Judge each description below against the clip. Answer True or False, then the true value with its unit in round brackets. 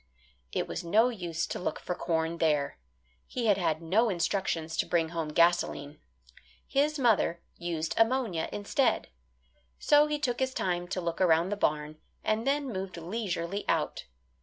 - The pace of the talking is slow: False (160 wpm)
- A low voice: False (180 Hz)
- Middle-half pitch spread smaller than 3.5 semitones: False (5.5 semitones)